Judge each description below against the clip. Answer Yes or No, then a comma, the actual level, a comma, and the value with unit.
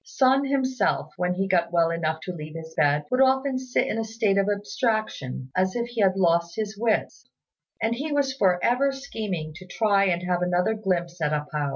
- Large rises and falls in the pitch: Yes, wide, 5.7 semitones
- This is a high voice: Yes, high, 195 Hz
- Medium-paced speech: No, fast, 210 wpm